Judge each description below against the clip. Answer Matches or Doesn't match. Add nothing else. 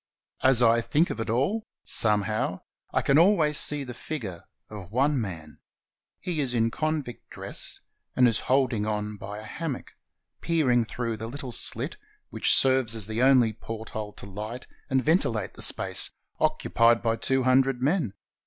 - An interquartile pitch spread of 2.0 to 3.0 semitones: Doesn't match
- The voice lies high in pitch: Doesn't match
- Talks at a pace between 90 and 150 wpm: Doesn't match